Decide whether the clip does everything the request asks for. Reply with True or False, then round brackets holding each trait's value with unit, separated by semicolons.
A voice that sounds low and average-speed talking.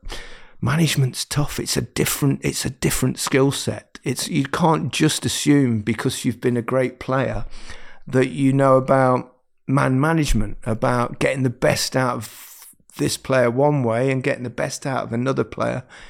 True (130 Hz; 170 wpm)